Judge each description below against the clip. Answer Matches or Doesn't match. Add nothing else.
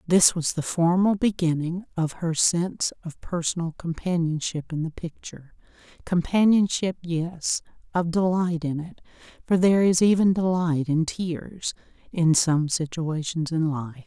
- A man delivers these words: Doesn't match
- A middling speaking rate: Doesn't match